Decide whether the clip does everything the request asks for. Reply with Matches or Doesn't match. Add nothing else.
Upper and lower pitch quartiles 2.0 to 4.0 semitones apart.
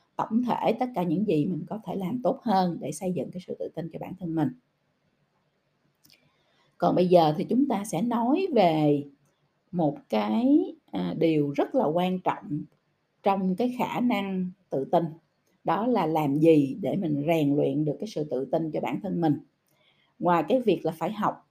Doesn't match